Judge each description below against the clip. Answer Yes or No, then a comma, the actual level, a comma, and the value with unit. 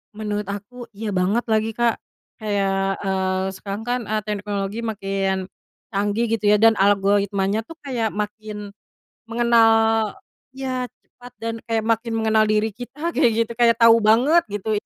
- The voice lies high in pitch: Yes, high, 215 Hz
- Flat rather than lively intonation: Yes, narrow, 2.3 semitones